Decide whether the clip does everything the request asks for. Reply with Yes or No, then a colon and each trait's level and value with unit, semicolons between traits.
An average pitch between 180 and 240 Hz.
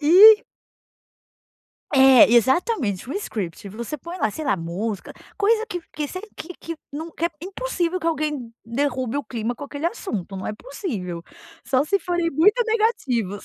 No: very high, 290 Hz